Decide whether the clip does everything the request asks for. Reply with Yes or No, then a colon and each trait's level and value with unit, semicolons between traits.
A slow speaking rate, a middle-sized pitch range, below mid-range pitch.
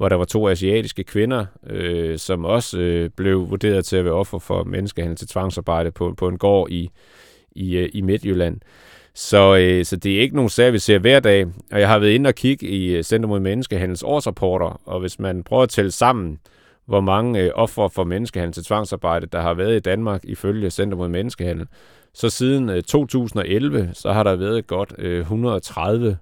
No: average, 200 wpm; average, 3.4 semitones; very low, 95 Hz